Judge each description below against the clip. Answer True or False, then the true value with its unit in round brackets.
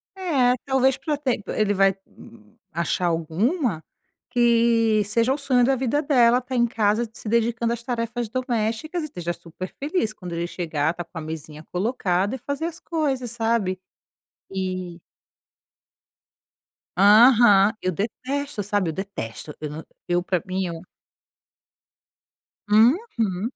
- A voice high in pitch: True (225 Hz)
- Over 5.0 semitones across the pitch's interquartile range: True (5.5 semitones)